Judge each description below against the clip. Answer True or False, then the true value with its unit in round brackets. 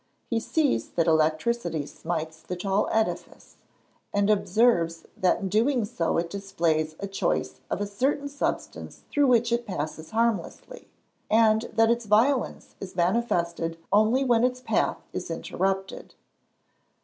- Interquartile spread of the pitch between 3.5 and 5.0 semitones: False (5.6 semitones)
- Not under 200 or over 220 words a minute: False (135 wpm)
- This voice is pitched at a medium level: False (205 Hz)